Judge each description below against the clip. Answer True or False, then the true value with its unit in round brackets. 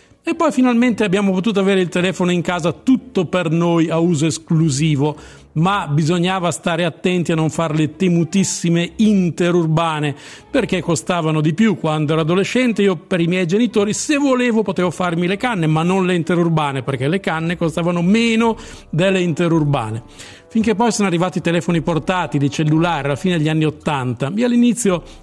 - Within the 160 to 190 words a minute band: True (170 wpm)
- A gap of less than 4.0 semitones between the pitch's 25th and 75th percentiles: True (3.5 semitones)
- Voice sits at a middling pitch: True (175 Hz)